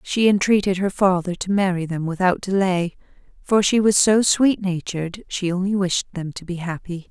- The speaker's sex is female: Yes, female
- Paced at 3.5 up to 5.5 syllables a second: Yes, 5.0 syllables/s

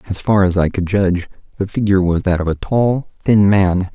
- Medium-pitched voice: No, very low, 95 Hz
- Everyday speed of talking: No, fast, 230 wpm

